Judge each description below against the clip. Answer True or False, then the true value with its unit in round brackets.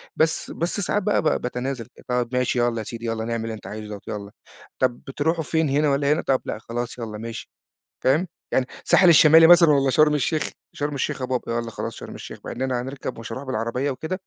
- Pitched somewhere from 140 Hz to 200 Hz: False (130 Hz)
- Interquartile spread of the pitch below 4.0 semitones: False (4.4 semitones)